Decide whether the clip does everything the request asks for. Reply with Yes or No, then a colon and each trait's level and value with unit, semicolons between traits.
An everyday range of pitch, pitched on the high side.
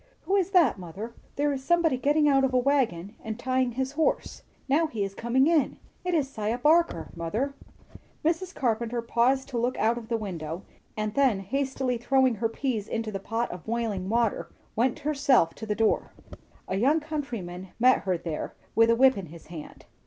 Yes: average, 4.5 semitones; high, 240 Hz